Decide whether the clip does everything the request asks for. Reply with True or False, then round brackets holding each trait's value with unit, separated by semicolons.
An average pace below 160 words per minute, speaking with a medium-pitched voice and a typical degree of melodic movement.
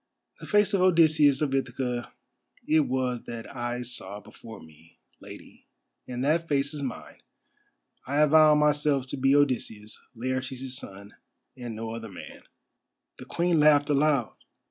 False (145 wpm; 130 Hz; 3.8 semitones)